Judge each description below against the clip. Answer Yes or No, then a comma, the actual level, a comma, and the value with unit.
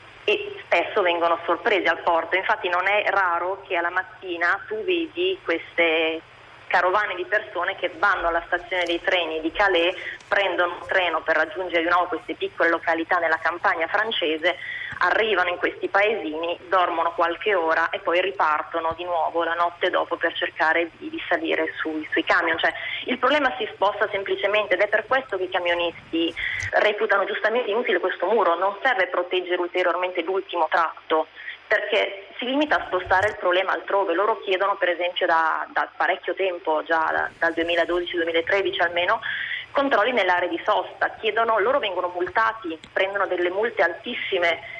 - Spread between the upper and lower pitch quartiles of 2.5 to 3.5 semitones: Yes, average, 2.9 semitones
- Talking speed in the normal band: Yes, average, 160 wpm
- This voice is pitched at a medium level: Yes, medium, 180 Hz